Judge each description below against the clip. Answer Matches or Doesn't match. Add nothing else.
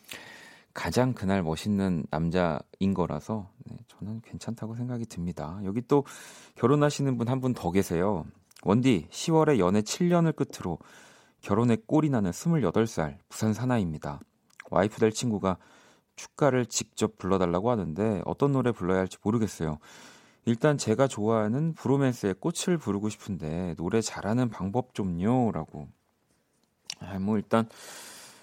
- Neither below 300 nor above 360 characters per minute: Doesn't match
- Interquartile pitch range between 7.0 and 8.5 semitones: Doesn't match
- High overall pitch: Doesn't match